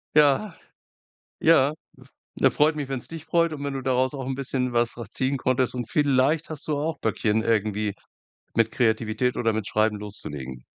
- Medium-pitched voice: No, low, 130 Hz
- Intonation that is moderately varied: Yes, average, 4.4 semitones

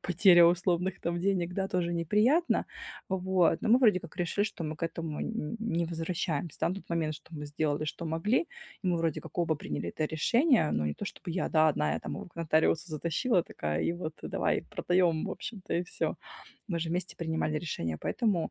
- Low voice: No, medium, 170 Hz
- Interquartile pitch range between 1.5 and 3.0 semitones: Yes, average, 2.7 semitones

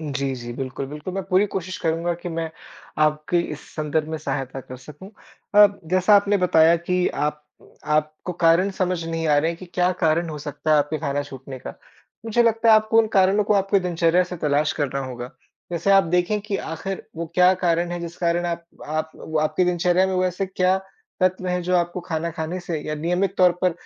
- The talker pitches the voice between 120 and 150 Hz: No, medium, 170 Hz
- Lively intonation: No, average, 3.3 semitones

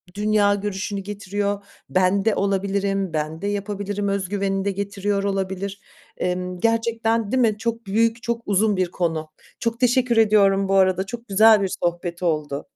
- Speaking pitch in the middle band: No, high, 200 Hz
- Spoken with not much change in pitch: Yes, narrow, 2.0 semitones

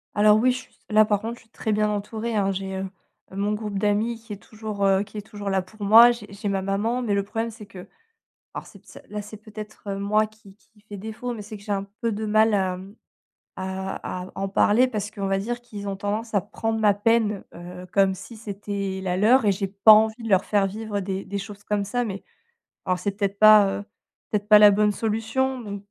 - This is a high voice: Yes, high, 210 Hz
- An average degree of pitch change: No, narrow, 1.8 semitones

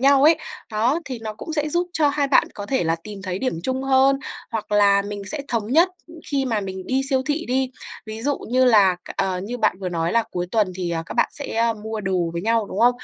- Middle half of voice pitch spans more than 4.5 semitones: Yes, average, 5.2 semitones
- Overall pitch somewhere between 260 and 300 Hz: No, high, 225 Hz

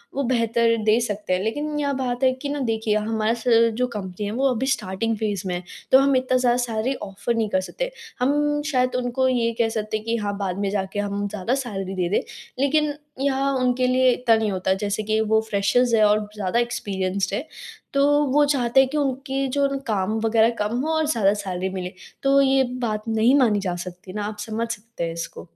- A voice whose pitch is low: No, high, 230 Hz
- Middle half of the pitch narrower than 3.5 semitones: No, average, 4.2 semitones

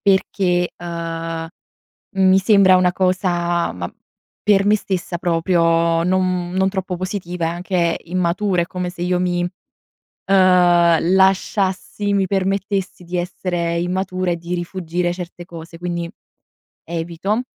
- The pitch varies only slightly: Yes, narrow, 1.7 semitones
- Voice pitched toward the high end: No, medium, 180 Hz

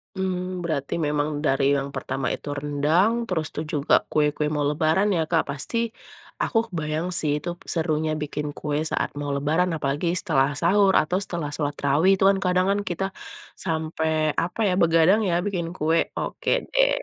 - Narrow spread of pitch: No, average, 3.5 semitones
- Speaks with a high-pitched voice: No, medium, 160 Hz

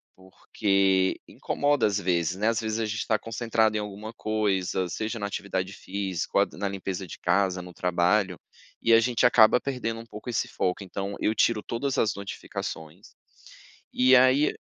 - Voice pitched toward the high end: No, low, 105 Hz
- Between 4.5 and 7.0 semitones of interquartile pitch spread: No, average, 3.3 semitones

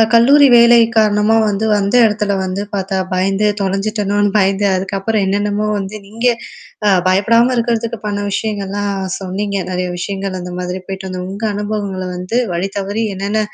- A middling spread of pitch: No, narrow, 2.0 semitones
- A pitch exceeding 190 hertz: Yes, high, 200 Hz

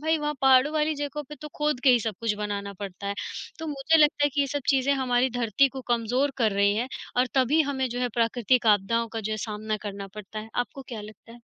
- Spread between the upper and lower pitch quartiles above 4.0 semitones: Yes, average, 4.6 semitones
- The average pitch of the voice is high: Yes, high, 245 Hz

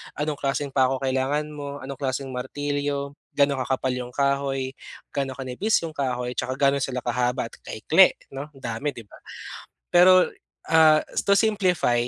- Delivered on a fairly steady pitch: Yes, narrow, 2.2 semitones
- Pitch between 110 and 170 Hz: Yes, medium, 140 Hz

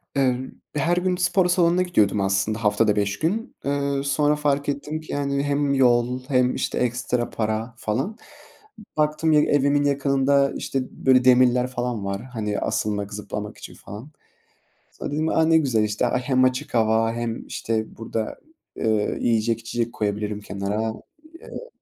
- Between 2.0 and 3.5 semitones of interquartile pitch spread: No, average, 4.7 semitones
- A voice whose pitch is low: Yes, low, 125 Hz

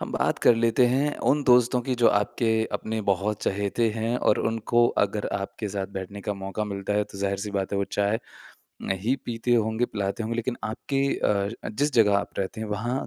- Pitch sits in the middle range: No, low, 110 Hz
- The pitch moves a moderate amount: Yes, average, 3.0 semitones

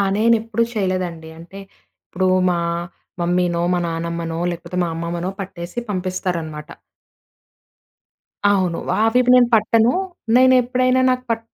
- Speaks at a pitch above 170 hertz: Yes, medium, 185 Hz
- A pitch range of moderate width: Yes, average, 4.9 semitones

